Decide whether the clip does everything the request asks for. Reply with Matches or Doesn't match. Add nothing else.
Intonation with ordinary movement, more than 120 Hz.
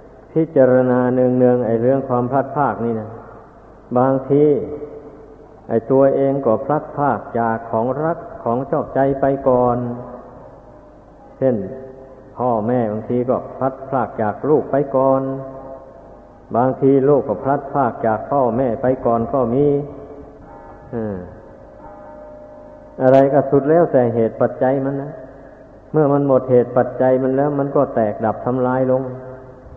Doesn't match